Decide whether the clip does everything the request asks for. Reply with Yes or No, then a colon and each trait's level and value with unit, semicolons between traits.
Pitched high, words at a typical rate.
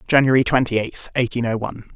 No: low, 120 Hz; average, 185 wpm